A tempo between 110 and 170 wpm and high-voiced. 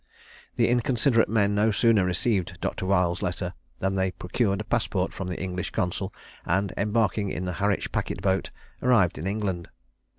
No: average, 165 wpm; very low, 95 Hz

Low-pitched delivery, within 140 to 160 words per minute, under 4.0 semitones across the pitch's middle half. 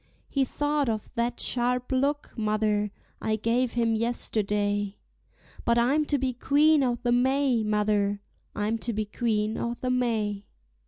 No: high, 235 Hz; average, 150 wpm; average, 3.2 semitones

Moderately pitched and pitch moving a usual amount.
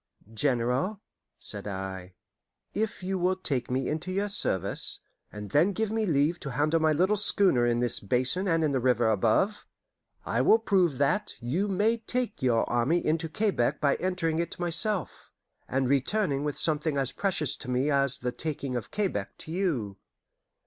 No: medium, 150 Hz; wide, 7.0 semitones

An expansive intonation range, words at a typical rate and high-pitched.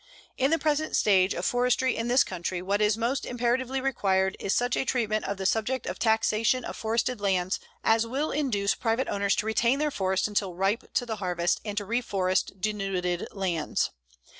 No: average, 4.3 semitones; average, 190 wpm; high, 215 Hz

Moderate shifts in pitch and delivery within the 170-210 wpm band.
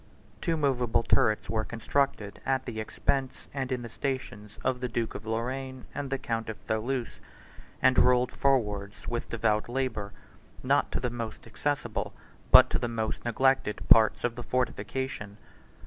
No: average, 3.1 semitones; average, 160 wpm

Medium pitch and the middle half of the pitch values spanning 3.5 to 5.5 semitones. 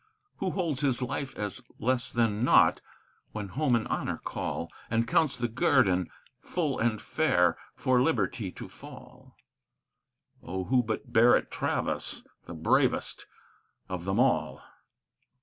No: low, 120 Hz; average, 4.3 semitones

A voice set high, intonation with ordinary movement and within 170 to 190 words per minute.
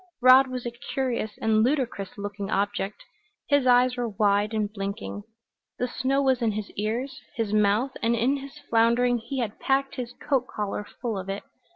Yes: high, 235 Hz; average, 3.7 semitones; average, 180 wpm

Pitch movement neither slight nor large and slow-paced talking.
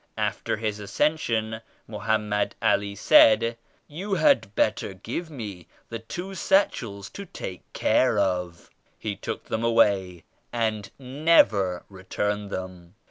Yes: average, 3.2 semitones; slow, 125 wpm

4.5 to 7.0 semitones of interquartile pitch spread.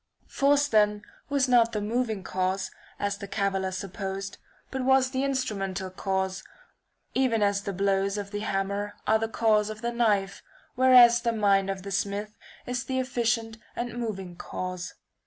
No: average, 3.5 semitones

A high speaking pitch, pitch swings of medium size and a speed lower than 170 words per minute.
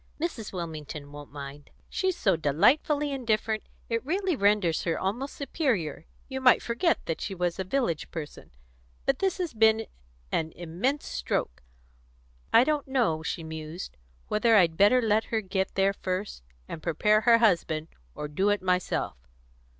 No: high, 200 Hz; wide, 7.2 semitones; average, 155 wpm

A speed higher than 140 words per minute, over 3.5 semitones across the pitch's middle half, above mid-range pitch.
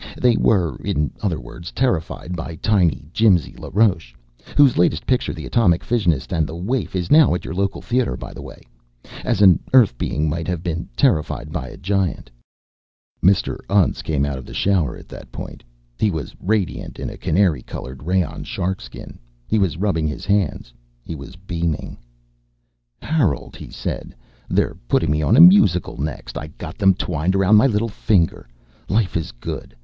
No: average, 175 wpm; average, 4.8 semitones; very low, 90 Hz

